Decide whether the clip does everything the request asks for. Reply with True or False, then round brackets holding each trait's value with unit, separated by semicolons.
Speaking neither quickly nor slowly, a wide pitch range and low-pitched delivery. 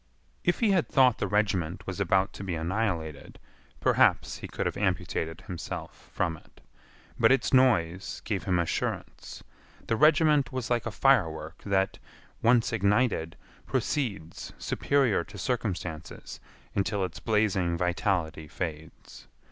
False (130 wpm; 5.8 semitones; 100 Hz)